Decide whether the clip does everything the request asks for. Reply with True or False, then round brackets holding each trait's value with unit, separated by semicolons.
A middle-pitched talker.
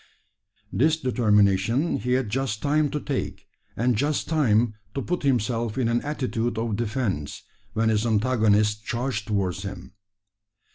False (115 Hz)